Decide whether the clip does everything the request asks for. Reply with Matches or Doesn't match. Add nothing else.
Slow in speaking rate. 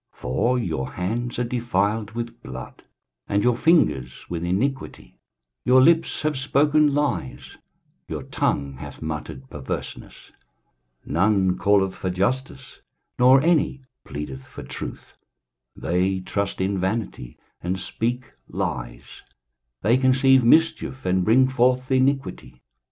Matches